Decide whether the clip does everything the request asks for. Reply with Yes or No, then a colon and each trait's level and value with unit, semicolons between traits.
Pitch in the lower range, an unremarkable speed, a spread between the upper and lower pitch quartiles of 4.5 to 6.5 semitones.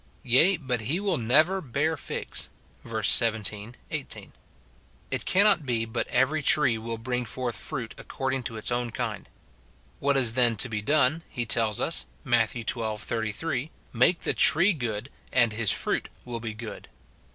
No: low, 120 Hz; average, 165 wpm; average, 3.9 semitones